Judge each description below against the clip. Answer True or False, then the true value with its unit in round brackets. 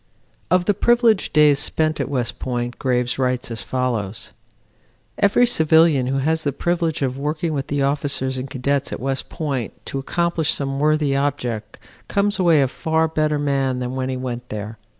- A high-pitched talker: False (140 Hz)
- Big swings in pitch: False (3.8 semitones)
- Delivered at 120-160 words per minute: False (175 wpm)